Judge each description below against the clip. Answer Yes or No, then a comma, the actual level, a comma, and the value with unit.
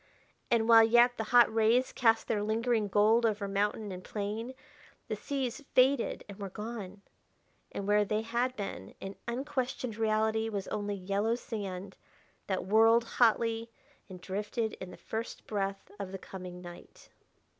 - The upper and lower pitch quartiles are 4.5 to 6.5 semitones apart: No, narrow, 2.6 semitones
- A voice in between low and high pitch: No, high, 220 Hz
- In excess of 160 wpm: No, average, 155 wpm